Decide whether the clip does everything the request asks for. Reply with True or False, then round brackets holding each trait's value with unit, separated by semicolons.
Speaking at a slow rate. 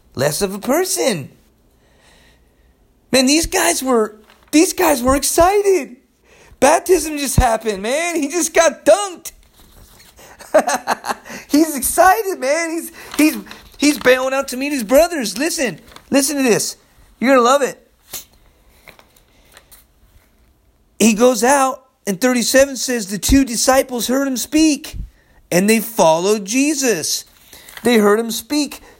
True (125 wpm)